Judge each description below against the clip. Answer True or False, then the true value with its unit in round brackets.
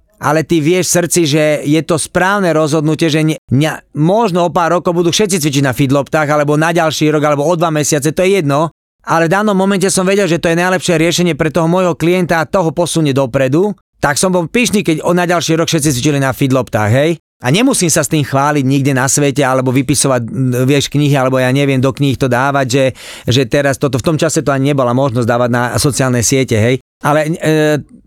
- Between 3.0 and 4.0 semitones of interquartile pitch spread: True (3.7 semitones)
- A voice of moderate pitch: True (155 Hz)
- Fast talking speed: True (220 wpm)